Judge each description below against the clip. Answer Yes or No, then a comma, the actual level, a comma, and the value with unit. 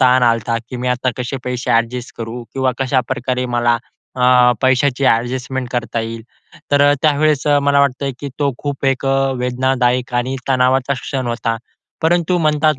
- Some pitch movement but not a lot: No, narrow, 2.1 semitones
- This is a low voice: Yes, low, 130 Hz